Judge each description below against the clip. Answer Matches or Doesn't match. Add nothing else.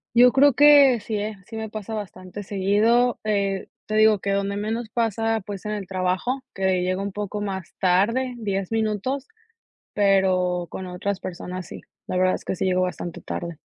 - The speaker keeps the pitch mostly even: Doesn't match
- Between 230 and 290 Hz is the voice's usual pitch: Doesn't match